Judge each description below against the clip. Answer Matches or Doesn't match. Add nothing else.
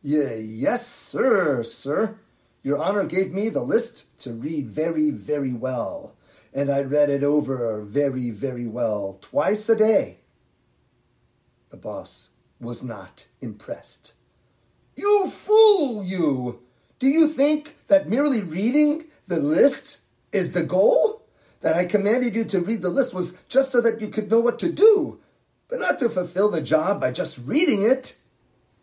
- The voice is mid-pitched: Matches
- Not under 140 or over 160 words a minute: Matches